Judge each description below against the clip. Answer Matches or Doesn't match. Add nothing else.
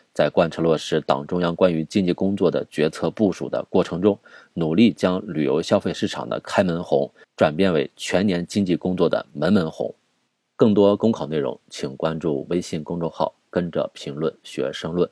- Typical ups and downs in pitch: Matches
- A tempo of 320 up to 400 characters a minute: Doesn't match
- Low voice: Matches